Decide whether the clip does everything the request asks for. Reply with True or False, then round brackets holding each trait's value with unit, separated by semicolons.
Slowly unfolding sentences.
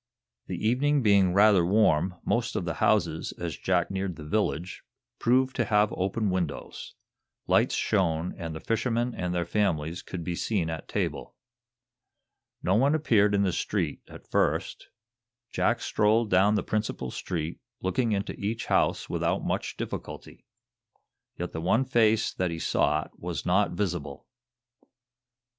False (150 wpm)